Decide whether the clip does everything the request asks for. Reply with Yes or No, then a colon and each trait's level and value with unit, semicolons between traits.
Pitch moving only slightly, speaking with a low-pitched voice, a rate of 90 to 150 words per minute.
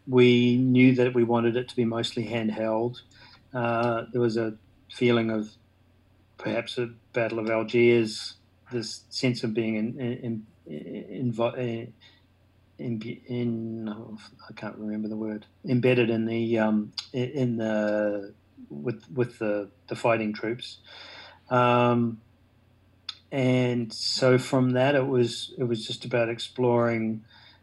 Yes: narrow, 2.1 semitones; low, 115 Hz; average, 140 wpm